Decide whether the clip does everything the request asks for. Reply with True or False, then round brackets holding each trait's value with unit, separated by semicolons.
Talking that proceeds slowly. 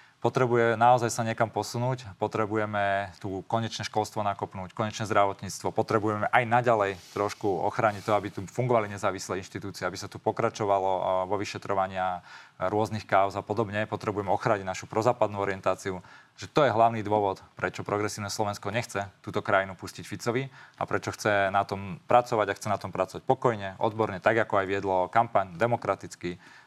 False (160 wpm)